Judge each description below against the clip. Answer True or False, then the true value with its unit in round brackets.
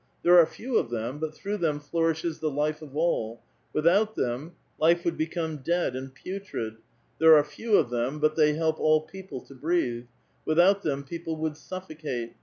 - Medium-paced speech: True (185 wpm)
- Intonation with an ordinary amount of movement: True (3.4 semitones)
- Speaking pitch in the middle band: True (155 Hz)